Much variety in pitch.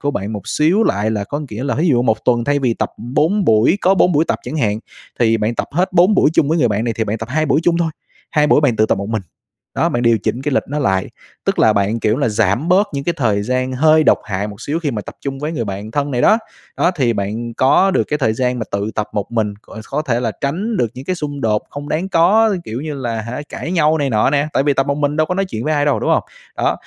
Yes: wide, 5.7 semitones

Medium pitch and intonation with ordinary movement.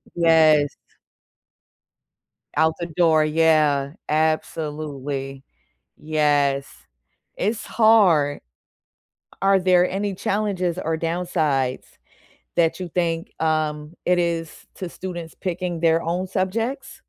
Yes: medium, 165 Hz; average, 3.0 semitones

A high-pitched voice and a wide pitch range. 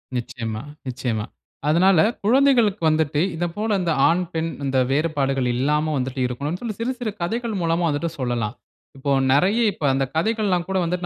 No: medium, 165 Hz; wide, 6.2 semitones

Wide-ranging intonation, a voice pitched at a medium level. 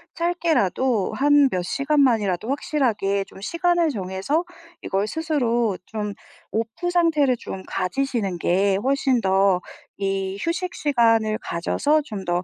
No: wide, 6.9 semitones; high, 230 Hz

